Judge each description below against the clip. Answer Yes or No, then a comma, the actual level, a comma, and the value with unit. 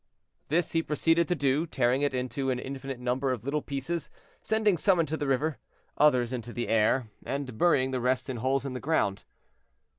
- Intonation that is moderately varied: Yes, average, 3.3 semitones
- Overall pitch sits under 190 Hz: Yes, low, 135 Hz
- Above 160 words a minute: Yes, average, 190 wpm